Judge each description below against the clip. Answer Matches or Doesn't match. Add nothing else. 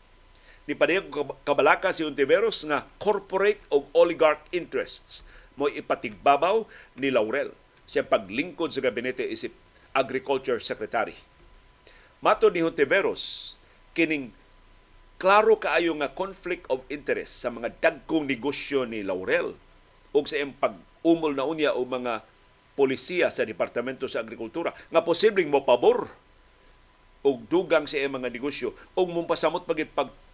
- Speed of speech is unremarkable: Matches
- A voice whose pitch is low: Doesn't match